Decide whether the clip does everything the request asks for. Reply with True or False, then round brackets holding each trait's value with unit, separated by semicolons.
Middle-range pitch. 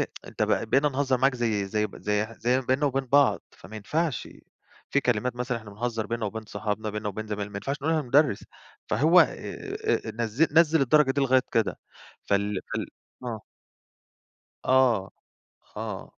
False (125 Hz)